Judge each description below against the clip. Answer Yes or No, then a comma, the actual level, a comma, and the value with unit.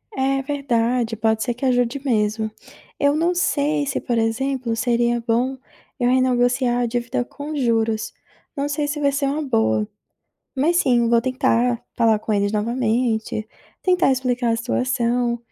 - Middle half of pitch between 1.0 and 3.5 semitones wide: Yes, average, 2.8 semitones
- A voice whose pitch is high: Yes, high, 245 Hz